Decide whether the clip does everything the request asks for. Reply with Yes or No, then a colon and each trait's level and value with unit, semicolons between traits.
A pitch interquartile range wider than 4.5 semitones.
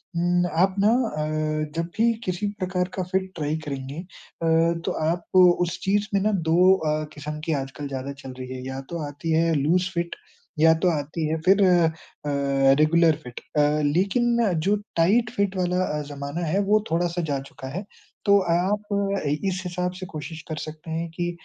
No: average, 3.5 semitones